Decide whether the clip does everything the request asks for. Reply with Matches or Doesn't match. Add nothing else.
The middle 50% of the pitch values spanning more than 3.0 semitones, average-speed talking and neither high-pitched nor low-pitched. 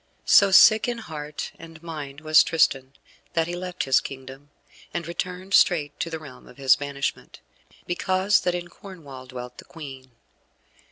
Matches